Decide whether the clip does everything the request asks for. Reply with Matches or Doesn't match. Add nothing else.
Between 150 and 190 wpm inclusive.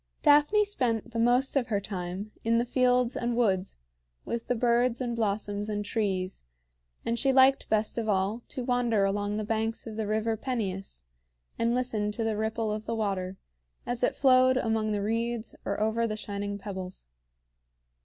Matches